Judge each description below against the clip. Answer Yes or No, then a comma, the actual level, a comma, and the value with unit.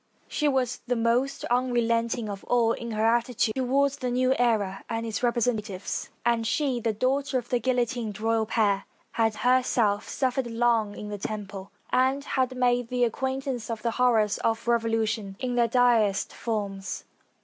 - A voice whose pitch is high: Yes, high, 235 Hz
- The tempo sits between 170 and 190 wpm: No, average, 160 wpm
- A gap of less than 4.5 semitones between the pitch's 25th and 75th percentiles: Yes, narrow, 2.4 semitones